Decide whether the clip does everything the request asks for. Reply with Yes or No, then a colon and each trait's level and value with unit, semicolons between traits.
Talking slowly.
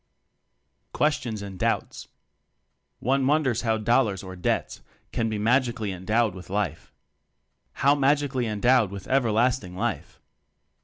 Yes: slow, 120 wpm